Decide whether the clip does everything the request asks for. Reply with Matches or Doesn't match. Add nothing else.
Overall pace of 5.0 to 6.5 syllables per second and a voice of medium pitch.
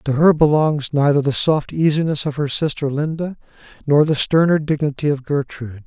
Matches